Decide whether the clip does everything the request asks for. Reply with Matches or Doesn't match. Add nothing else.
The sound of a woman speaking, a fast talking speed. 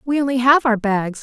Matches